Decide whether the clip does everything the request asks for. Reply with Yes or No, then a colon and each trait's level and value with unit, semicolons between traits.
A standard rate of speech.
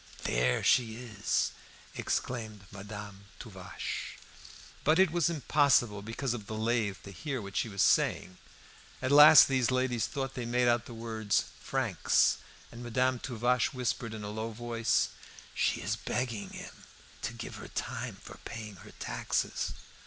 Yes: average, 150 wpm